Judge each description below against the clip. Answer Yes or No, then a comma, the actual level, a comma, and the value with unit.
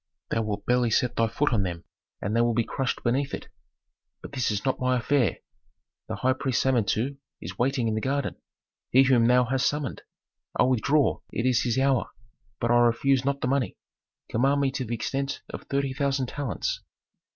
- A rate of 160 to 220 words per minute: Yes, average, 195 wpm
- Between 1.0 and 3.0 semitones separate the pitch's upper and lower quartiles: Yes, average, 2.7 semitones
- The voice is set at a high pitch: No, low, 125 Hz